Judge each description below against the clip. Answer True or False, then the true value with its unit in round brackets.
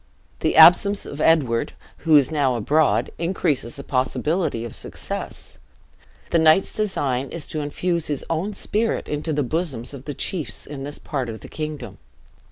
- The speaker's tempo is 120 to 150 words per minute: False (165 wpm)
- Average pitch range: True (3.9 semitones)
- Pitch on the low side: False (150 Hz)